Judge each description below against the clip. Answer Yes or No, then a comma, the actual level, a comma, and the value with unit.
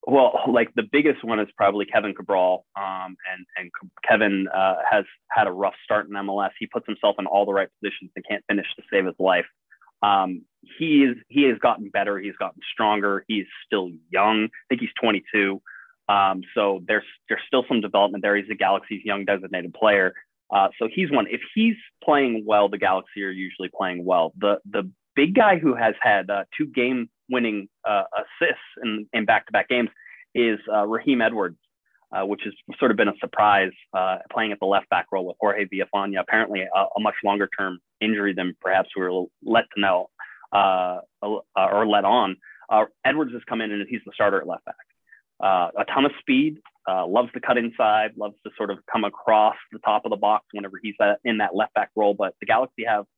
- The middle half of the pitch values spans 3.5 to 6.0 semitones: No, average, 2.8 semitones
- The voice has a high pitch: No, low, 100 Hz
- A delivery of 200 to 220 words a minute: Yes, fast, 205 wpm